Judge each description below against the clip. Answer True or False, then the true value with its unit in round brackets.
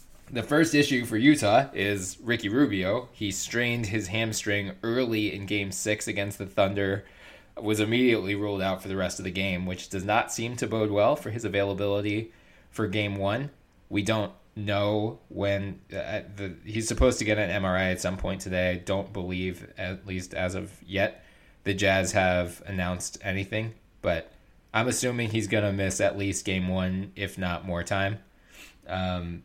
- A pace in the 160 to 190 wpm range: True (175 wpm)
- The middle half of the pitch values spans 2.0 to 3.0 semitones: True (2.6 semitones)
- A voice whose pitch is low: True (100 Hz)